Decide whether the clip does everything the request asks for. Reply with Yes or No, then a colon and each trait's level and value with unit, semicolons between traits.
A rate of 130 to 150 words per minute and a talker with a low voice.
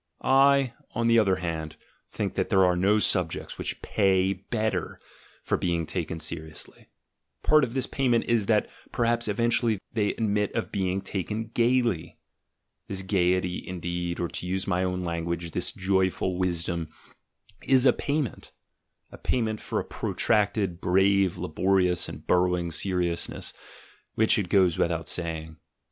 Yes: average, 145 wpm; very low, 95 Hz